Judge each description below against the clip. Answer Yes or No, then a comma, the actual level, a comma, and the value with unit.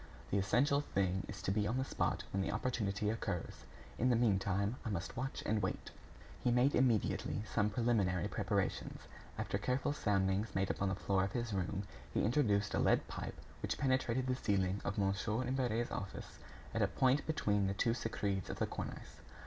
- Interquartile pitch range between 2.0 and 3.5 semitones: No, average, 4.1 semitones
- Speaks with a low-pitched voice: Yes, low, 105 Hz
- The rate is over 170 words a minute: Yes, average, 185 wpm